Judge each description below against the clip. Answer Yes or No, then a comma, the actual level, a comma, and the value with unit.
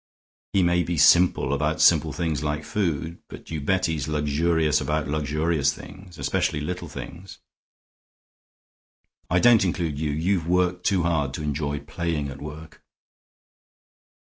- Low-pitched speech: Yes, very low, 80 Hz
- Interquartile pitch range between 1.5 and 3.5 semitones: Yes, average, 2.9 semitones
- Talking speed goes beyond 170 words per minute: No, average, 140 wpm